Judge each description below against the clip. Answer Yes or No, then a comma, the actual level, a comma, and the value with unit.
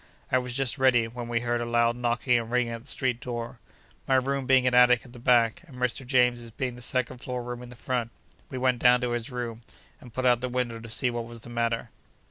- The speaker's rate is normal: No, fast, 255 wpm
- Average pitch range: No, narrow, 1.2 semitones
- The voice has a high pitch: No, low, 125 Hz